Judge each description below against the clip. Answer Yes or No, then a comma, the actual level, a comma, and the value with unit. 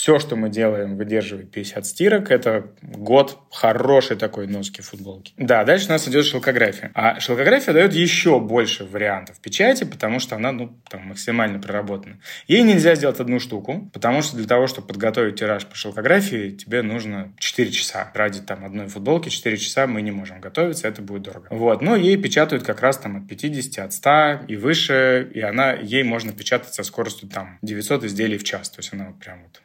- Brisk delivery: Yes, fast, 190 wpm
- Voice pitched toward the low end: Yes, low, 110 Hz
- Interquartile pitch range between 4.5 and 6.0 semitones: Yes, average, 5.0 semitones